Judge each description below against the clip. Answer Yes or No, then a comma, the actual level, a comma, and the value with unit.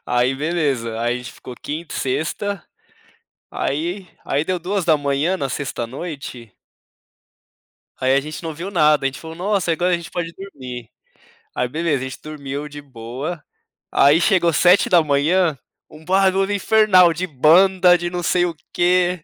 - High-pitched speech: No, medium, 160 Hz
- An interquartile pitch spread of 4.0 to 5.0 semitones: Yes, average, 4.6 semitones